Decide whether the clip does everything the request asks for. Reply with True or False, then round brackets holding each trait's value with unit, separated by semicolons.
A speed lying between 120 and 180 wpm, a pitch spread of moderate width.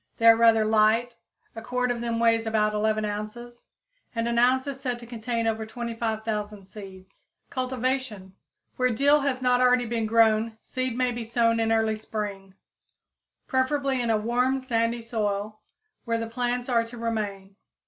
False (165 wpm; 2.2 semitones)